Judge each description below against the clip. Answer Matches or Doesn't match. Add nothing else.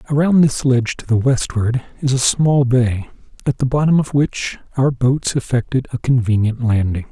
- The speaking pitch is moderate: Doesn't match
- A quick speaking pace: Doesn't match